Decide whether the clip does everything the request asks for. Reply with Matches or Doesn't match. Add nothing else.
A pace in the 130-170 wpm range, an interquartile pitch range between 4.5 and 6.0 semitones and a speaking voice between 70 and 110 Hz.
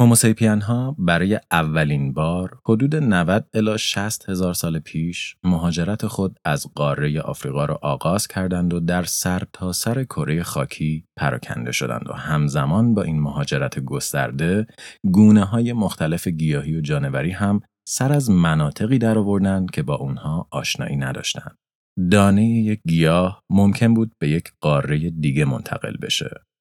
Matches